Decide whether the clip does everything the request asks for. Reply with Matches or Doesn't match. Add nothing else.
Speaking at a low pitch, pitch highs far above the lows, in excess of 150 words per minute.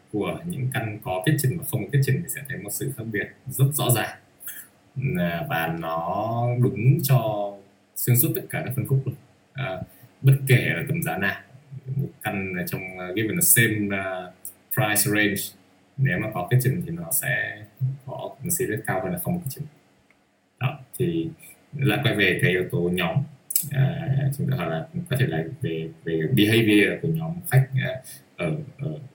Matches